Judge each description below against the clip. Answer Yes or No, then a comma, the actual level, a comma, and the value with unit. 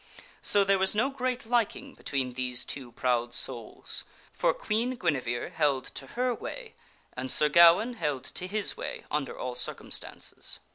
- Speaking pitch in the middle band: Yes, medium, 165 Hz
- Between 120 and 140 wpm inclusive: No, average, 155 wpm